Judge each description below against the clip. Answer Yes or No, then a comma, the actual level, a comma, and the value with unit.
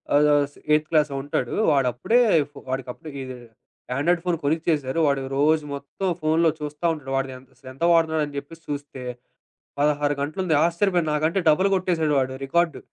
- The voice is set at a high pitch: No, medium, 150 Hz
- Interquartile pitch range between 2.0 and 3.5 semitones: Yes, average, 2.9 semitones